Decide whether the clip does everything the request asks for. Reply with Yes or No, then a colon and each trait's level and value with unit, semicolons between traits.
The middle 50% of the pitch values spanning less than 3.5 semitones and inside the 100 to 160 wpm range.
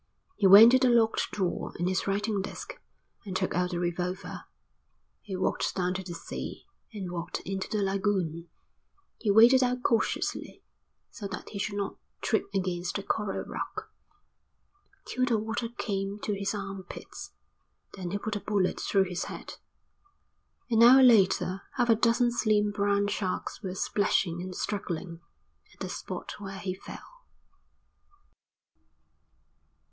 Yes: average, 3.0 semitones; average, 150 wpm